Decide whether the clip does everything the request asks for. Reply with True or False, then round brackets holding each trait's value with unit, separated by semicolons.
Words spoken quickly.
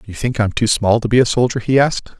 True (330 wpm)